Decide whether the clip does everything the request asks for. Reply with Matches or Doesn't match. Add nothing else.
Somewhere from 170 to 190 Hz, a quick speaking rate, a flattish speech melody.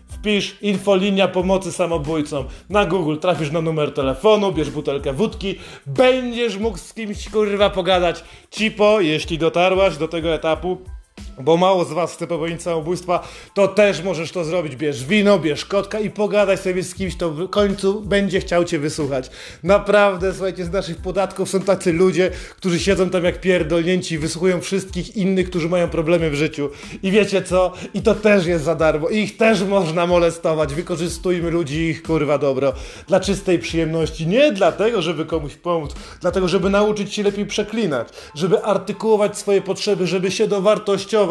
Doesn't match